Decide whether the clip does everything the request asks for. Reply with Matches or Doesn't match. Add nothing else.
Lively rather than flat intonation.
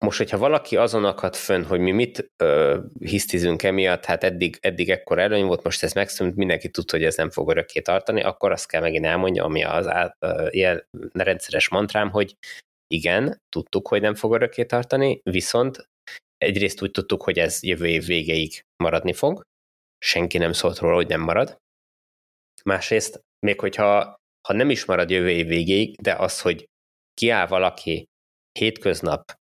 Matches